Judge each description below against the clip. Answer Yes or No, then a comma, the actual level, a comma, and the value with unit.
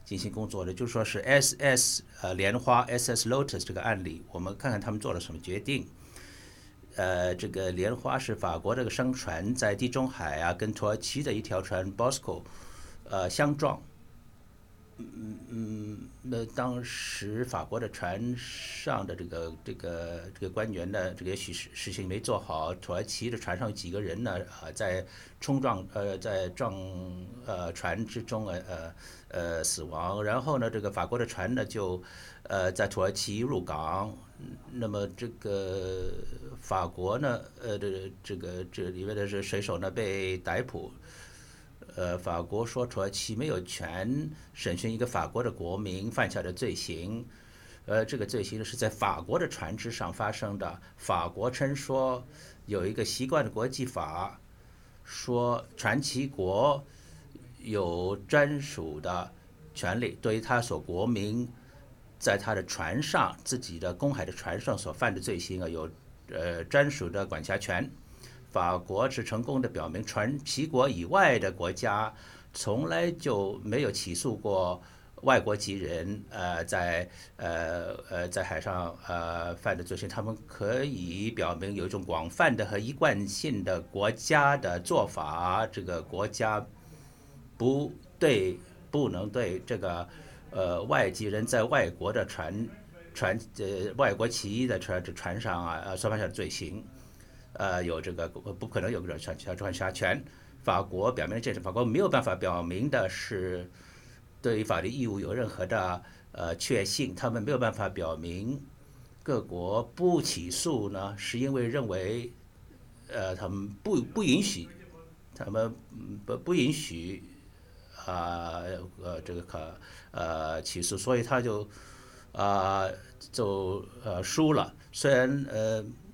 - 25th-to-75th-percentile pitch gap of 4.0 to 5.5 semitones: Yes, average, 4.8 semitones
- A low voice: Yes, low, 100 Hz